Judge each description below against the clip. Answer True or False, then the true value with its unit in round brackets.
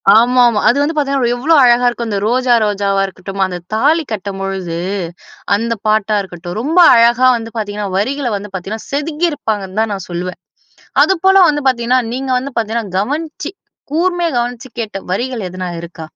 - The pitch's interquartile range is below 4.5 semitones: False (5.3 semitones)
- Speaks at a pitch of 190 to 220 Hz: False (230 Hz)